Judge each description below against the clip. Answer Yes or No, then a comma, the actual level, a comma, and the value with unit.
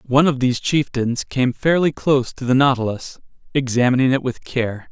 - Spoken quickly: No, average, 170 wpm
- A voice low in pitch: Yes, low, 130 Hz